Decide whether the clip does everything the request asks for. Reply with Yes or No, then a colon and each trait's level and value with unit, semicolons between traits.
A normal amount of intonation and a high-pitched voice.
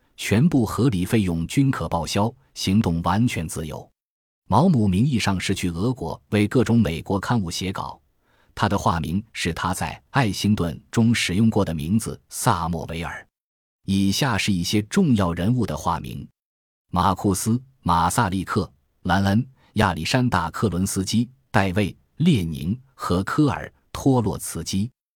No: average, 4.8 semitones; low, 100 Hz